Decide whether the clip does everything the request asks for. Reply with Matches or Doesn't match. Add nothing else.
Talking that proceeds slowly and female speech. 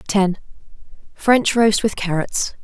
Matches